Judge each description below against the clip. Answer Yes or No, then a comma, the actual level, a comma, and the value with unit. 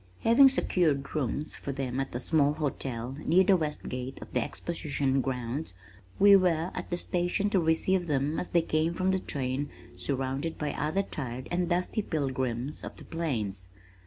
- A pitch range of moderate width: Yes, average, 4.8 semitones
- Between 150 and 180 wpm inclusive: Yes, average, 175 wpm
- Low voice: No, medium, 150 Hz